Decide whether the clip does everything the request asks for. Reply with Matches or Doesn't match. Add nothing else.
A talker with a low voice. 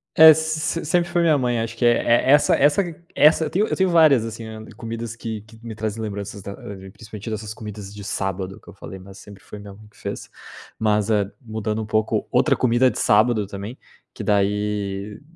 Matches